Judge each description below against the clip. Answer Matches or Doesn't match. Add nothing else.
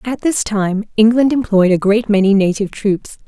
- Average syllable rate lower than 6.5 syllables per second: Matches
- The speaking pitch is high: Matches